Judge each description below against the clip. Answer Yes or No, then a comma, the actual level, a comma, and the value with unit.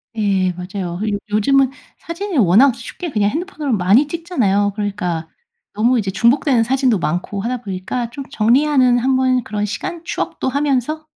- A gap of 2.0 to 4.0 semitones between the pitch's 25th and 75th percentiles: No, average, 5.3 semitones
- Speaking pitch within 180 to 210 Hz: No, high, 235 Hz